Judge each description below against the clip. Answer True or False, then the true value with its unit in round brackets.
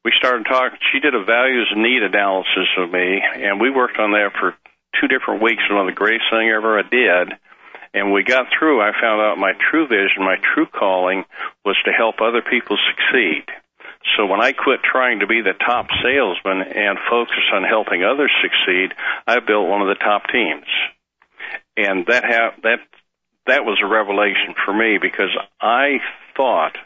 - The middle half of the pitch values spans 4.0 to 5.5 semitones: False (3.2 semitones)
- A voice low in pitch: True (105 Hz)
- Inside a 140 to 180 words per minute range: False (190 wpm)